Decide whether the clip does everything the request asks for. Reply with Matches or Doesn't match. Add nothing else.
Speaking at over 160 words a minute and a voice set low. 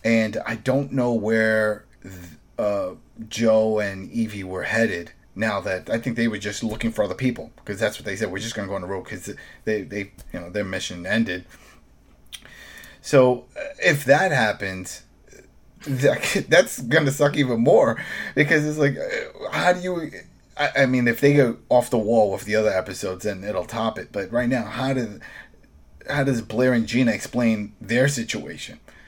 Matches